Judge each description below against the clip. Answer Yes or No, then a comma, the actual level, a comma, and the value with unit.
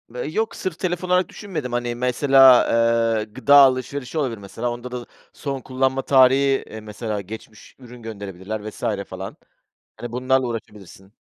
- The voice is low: Yes, low, 125 Hz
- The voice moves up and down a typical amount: Yes, average, 3.7 semitones